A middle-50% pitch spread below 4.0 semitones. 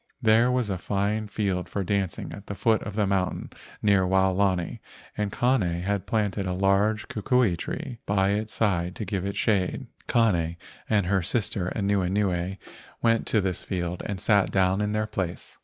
Yes: narrow, 2.5 semitones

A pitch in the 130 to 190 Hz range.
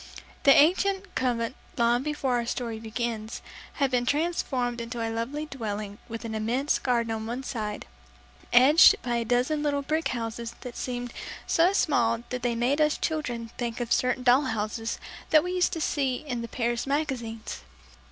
No: high, 245 Hz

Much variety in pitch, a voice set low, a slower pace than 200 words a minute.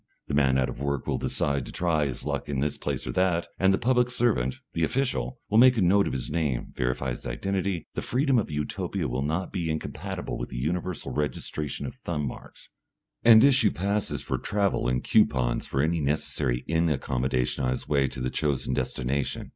No: wide, 6.7 semitones; very low, 75 Hz; fast, 205 wpm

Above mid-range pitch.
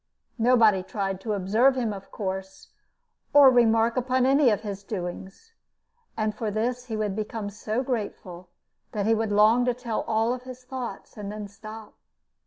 Yes: high, 220 Hz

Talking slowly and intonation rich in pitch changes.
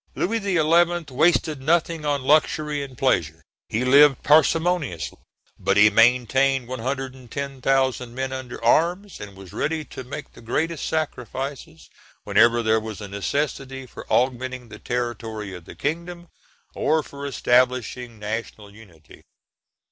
No: slow, 130 wpm; average, 4.4 semitones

